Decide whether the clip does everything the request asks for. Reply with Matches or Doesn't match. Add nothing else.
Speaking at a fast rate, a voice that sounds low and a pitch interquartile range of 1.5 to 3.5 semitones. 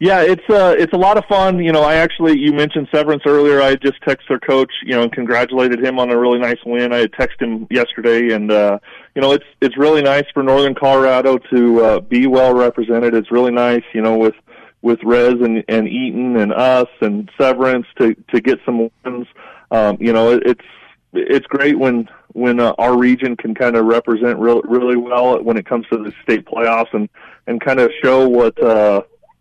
Matches